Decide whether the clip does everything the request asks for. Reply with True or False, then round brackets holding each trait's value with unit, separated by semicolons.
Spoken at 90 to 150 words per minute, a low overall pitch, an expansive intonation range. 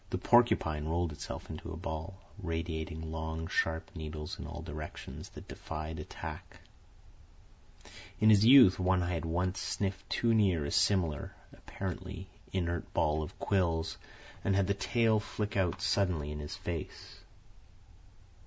False (145 wpm; 85 Hz; 3.5 semitones)